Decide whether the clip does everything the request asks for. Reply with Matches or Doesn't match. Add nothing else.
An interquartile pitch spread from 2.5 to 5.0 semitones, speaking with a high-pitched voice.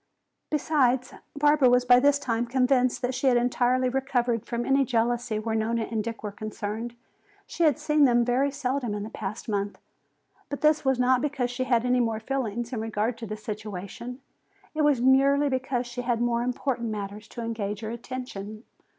Matches